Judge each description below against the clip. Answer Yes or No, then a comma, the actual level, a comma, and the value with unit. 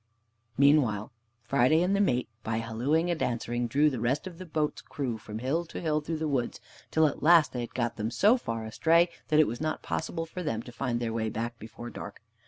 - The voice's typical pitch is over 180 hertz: No, low, 130 Hz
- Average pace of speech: No, fast, 225 wpm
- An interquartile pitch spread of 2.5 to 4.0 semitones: No, average, 5.2 semitones